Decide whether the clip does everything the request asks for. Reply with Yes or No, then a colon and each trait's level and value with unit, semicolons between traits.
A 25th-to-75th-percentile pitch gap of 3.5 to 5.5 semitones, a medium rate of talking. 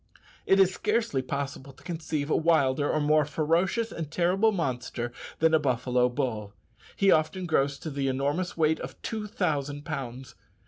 Yes: average, 4.4 semitones; average, 165 wpm